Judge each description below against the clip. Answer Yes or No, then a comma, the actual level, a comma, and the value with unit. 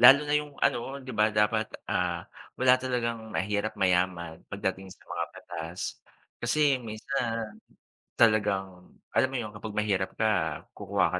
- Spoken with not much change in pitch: No, average, 3.8 semitones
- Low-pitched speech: Yes, low, 105 Hz